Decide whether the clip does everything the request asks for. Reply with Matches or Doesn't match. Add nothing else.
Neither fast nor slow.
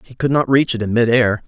Doesn't match